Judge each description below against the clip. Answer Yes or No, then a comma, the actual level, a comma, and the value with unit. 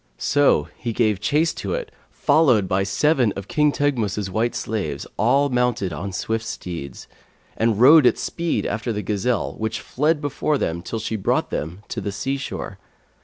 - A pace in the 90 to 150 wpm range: No, average, 170 wpm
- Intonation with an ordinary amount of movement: No, wide, 6.2 semitones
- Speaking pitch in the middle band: No, low, 115 Hz